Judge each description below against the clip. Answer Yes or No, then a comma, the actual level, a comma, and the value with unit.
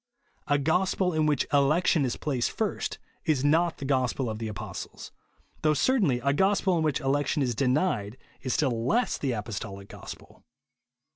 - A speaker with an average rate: Yes, average, 160 wpm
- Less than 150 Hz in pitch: Yes, medium, 140 Hz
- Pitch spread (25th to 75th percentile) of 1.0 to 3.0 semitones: No, average, 4.3 semitones